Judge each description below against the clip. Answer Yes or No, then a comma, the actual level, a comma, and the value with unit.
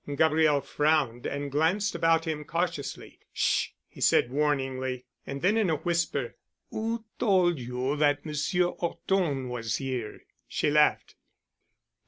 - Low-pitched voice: No, medium, 150 Hz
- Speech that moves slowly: Yes, slow, 130 wpm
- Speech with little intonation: No, average, 4.2 semitones